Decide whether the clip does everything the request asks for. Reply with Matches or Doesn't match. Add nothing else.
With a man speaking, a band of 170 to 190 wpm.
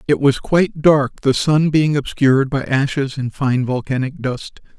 Matches